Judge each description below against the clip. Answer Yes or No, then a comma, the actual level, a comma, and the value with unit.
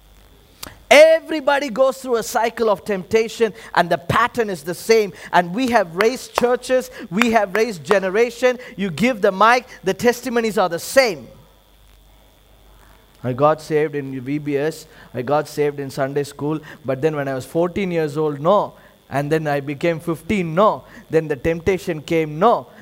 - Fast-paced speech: No, average, 165 wpm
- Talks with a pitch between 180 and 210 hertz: Yes, high, 190 Hz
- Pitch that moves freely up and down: Yes, wide, 7.1 semitones